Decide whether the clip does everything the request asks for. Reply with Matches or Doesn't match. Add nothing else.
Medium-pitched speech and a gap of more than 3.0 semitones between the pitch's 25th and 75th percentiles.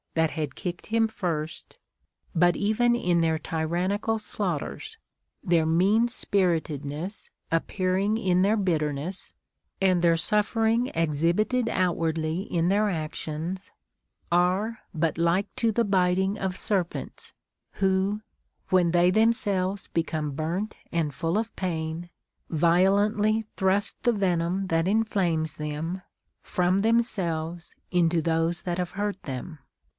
Matches